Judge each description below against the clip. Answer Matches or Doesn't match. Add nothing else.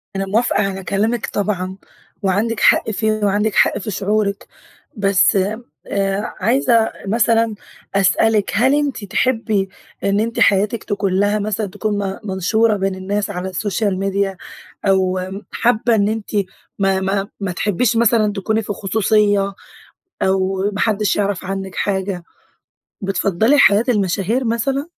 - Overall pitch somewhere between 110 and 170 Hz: Doesn't match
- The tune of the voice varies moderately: Doesn't match